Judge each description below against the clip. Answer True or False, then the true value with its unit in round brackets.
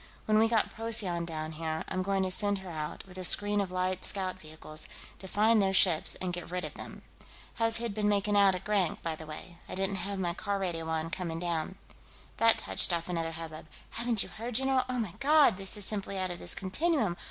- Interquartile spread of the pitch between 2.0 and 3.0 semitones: False (3.6 semitones)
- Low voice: False (190 Hz)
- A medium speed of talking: False (230 wpm)